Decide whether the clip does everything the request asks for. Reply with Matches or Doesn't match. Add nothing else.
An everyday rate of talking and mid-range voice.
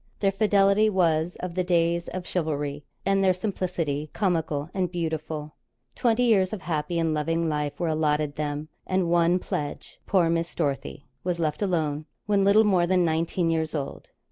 Matches